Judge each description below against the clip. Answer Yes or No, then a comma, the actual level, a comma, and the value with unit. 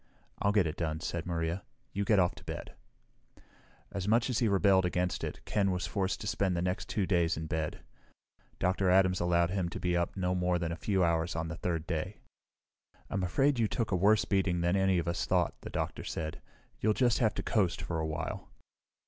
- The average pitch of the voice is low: Yes, very low, 90 Hz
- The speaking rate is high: Yes, fast, 215 wpm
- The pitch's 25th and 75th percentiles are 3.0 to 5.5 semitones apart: No, narrow, 2.6 semitones